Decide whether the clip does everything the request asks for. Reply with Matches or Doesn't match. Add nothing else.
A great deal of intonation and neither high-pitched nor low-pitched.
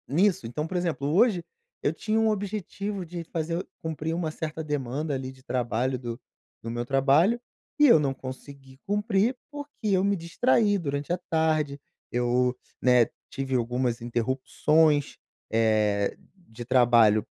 Matches